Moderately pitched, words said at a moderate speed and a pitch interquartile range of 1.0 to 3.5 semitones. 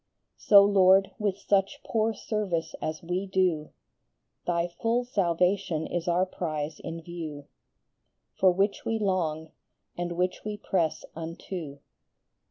No: medium, 180 Hz; slow, 130 wpm; average, 3.2 semitones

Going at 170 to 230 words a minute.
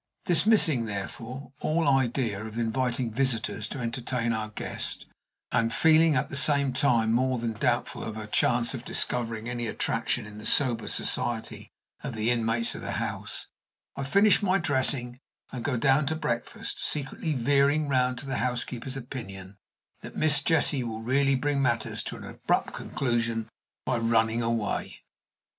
No: average, 155 wpm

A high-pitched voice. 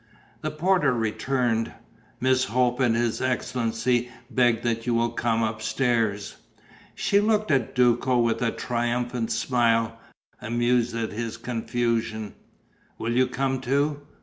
No: low, 120 Hz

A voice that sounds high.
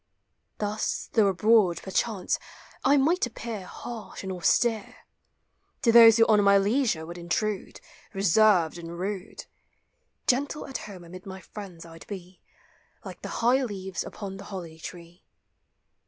Yes: high, 200 Hz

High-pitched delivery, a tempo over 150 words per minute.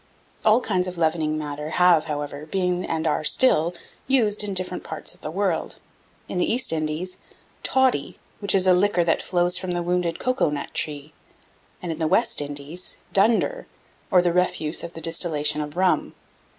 No: medium, 175 Hz; average, 175 wpm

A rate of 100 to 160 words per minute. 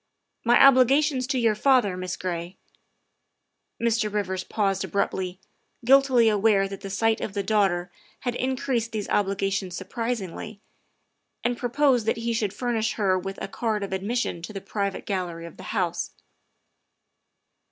Yes: average, 150 wpm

